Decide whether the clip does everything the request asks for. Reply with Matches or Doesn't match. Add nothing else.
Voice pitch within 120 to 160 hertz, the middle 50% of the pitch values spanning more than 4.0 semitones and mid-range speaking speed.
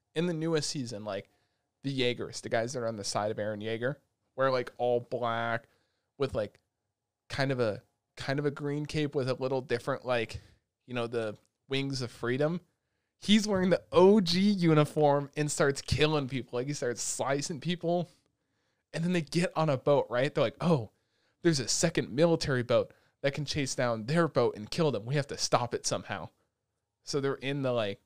Matches